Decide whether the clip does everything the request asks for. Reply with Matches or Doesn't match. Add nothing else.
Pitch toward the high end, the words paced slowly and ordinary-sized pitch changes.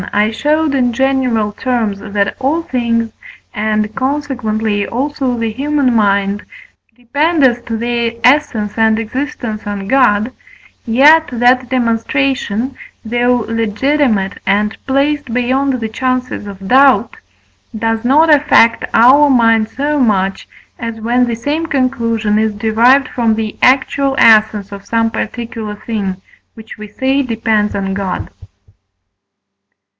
Matches